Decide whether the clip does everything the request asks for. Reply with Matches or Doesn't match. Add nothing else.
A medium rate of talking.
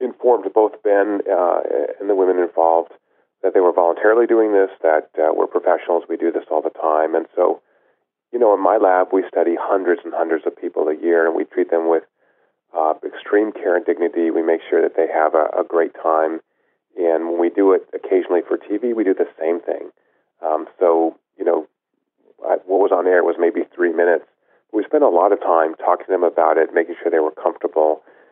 Doesn't match